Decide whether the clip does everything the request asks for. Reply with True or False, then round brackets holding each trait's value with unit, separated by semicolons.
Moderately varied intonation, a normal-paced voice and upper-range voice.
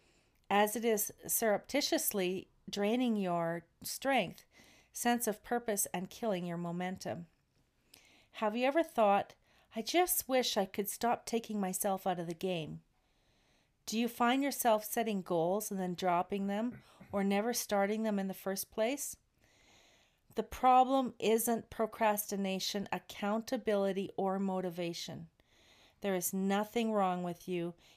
False (3.6 semitones; 130 wpm; 205 Hz)